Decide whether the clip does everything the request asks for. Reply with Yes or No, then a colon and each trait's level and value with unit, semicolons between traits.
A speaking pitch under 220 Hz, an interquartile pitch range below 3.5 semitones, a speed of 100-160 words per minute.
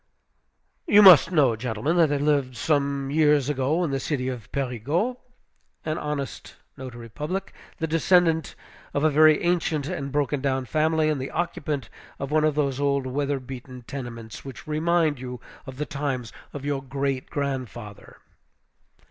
Yes: medium, 140 Hz; average, 2.9 semitones; average, 155 wpm